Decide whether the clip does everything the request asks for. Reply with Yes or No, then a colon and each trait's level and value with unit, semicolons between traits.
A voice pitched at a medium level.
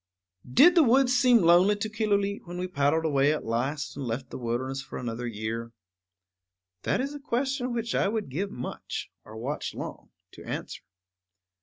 Yes: medium, 170 Hz